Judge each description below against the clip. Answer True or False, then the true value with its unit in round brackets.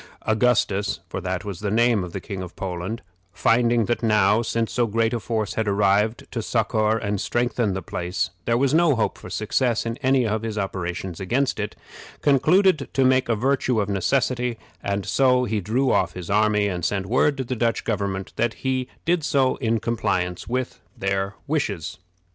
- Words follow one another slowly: False (190 wpm)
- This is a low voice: True (110 Hz)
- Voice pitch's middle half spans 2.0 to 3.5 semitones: False (3.9 semitones)